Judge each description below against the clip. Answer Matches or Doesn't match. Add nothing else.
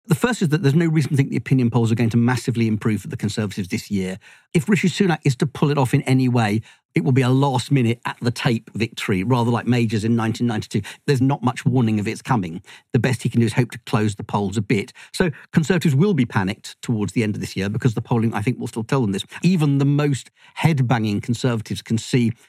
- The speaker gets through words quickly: Matches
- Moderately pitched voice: Doesn't match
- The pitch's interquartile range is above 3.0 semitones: Matches